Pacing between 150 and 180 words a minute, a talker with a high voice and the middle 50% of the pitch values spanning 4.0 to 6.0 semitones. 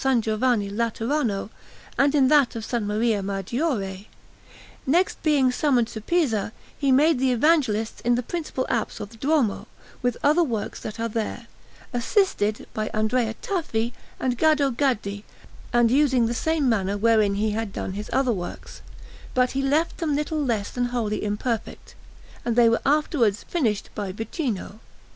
Yes: average, 160 wpm; high, 235 Hz; average, 4.6 semitones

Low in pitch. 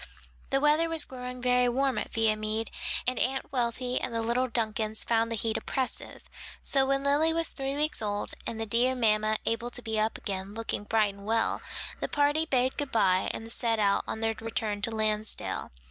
No: high, 230 Hz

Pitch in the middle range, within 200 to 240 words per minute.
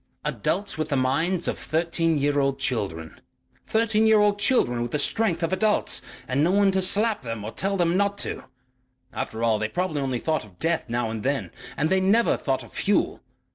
Yes: medium, 160 Hz; fast, 205 wpm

